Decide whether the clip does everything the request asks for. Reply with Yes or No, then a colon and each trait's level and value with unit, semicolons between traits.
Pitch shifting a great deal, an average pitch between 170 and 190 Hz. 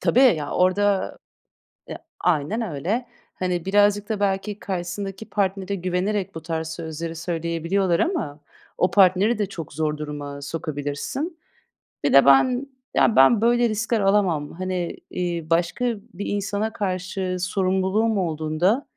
No: average, 3.9 semitones; medium, 185 Hz